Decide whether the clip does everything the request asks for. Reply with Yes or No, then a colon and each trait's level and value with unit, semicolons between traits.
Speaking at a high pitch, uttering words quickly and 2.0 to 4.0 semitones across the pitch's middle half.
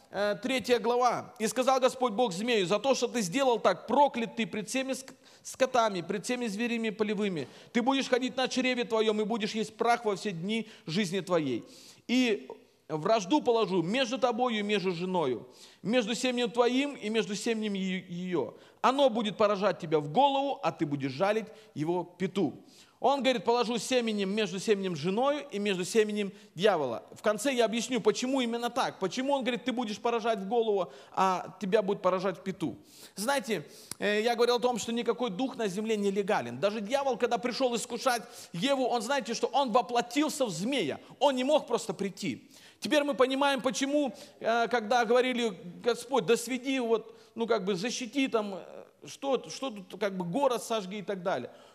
Yes: high, 230 Hz; fast, 175 wpm; average, 3.5 semitones